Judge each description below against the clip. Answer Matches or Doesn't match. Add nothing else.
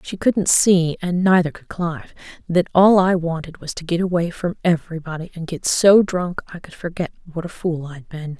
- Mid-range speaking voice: Matches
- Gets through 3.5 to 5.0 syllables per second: Doesn't match